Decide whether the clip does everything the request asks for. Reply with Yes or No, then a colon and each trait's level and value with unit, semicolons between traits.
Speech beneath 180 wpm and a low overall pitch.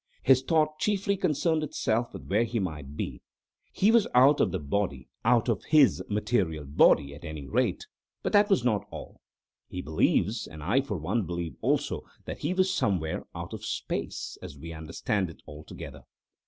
Yes: average, 170 wpm; low, 105 Hz